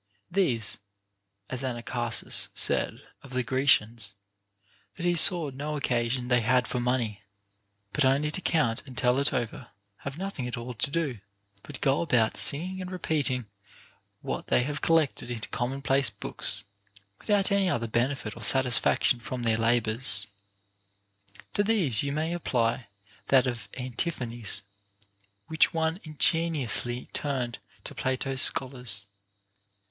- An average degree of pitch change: Yes, average, 4.2 semitones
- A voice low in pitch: Yes, low, 130 Hz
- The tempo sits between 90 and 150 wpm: Yes, average, 140 wpm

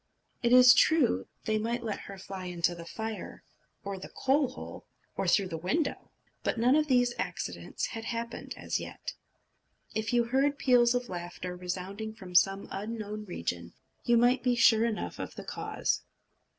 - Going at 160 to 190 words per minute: Yes, average, 170 wpm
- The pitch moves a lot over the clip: No, average, 4.5 semitones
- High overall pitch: Yes, high, 220 Hz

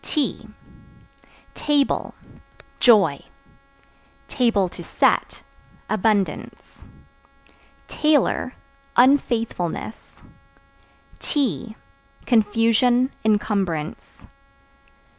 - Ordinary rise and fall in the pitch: Yes, average, 3.6 semitones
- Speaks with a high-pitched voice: Yes, high, 225 Hz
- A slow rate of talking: Yes, slow, 45 wpm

